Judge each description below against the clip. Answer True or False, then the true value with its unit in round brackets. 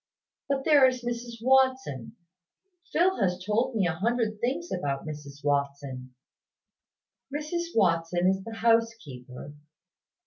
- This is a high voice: True (215 Hz)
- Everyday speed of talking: False (115 wpm)